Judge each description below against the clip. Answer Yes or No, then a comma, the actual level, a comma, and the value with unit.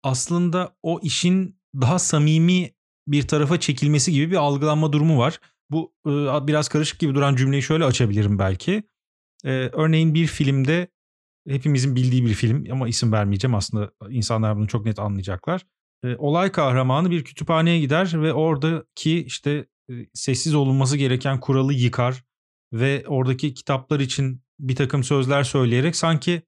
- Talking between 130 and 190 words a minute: Yes, average, 135 wpm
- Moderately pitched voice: Yes, medium, 145 Hz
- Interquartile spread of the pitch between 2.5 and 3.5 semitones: No, average, 3.9 semitones